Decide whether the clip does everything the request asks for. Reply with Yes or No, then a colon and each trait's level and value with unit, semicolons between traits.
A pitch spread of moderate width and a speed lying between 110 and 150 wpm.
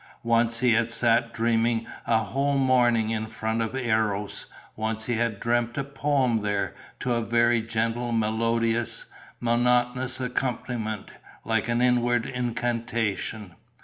No: narrow, 1.5 semitones; slow, 135 wpm